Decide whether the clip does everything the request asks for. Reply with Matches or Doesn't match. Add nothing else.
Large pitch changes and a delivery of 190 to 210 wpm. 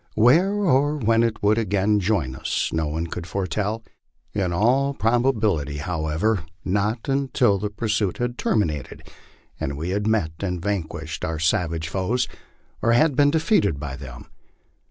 Doesn't match